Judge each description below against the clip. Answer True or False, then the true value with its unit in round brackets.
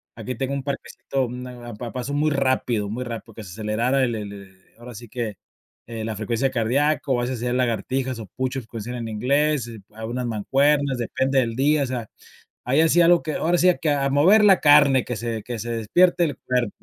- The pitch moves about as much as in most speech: True (3.3 semitones)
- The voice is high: False (125 Hz)